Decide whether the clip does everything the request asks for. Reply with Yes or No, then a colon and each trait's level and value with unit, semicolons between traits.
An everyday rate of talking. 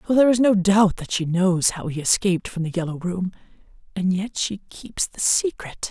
No: fast, 215 wpm